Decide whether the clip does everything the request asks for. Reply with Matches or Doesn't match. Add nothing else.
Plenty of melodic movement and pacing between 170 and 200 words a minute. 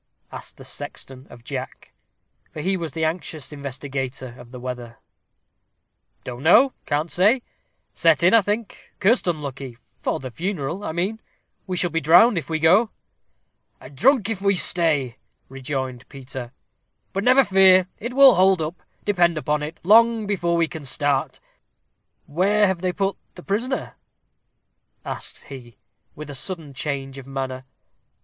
Doesn't match